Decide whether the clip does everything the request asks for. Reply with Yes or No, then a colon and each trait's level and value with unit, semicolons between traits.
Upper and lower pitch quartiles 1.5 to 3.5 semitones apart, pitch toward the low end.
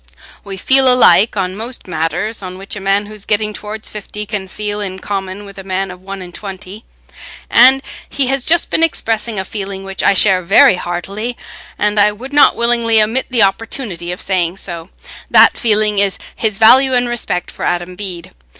No: average, 3.1 semitones; high, 205 Hz